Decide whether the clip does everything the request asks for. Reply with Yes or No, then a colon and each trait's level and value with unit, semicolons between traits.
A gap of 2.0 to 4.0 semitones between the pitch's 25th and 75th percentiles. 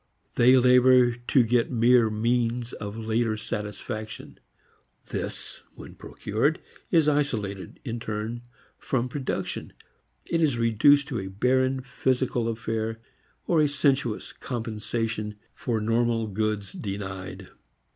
Yes: average, 2.7 semitones